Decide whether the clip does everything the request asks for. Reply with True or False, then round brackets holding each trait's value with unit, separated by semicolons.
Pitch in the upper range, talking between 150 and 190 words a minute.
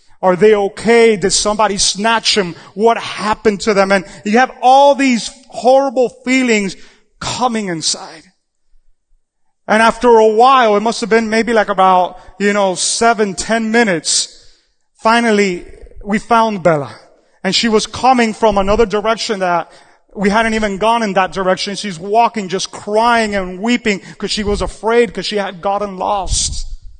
True (210 Hz; 155 wpm)